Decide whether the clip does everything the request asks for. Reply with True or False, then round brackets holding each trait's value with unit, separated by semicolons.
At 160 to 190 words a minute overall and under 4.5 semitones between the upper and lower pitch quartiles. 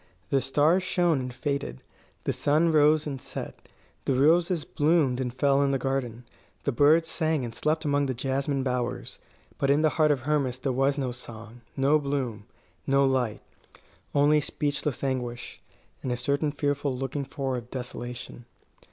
True (165 wpm; 2.7 semitones)